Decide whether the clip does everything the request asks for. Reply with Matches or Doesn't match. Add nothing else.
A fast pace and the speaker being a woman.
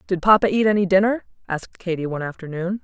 Doesn't match